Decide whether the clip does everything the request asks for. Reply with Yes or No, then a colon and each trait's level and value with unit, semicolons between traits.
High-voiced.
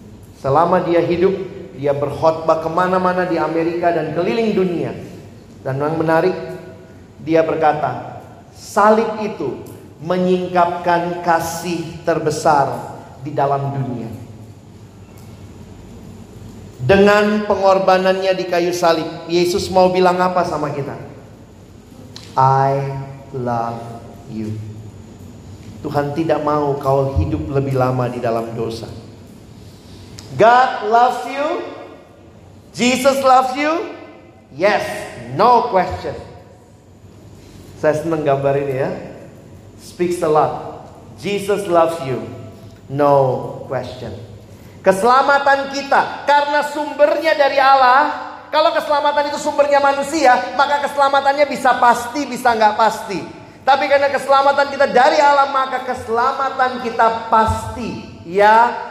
No: medium, 165 Hz